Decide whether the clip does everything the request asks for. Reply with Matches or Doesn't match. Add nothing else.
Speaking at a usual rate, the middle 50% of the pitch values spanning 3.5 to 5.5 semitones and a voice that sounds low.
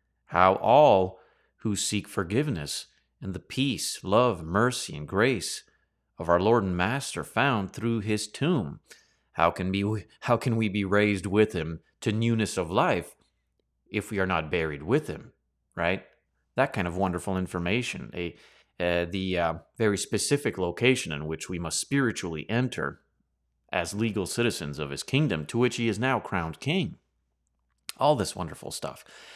Matches